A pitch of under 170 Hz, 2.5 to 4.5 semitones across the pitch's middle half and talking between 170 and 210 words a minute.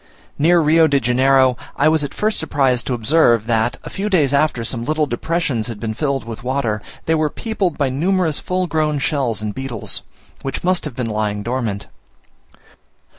No: low, 135 Hz; average, 5.2 semitones; average, 180 wpm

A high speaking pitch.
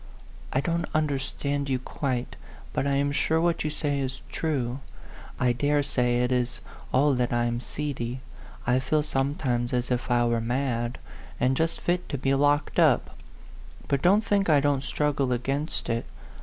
No: low, 135 Hz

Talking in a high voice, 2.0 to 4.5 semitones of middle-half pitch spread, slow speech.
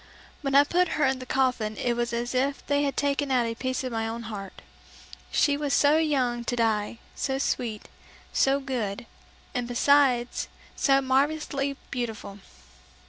No: very high, 255 Hz; average, 3.0 semitones; average, 165 wpm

